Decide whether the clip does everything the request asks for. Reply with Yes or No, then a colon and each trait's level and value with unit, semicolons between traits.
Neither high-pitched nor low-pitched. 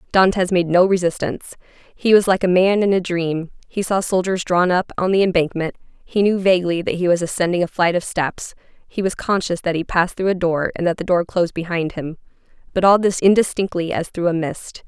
Yes: medium, 180 Hz